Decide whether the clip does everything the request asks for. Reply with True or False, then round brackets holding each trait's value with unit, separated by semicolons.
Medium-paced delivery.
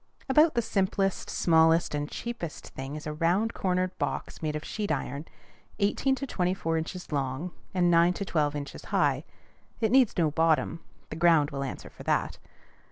True (175 wpm)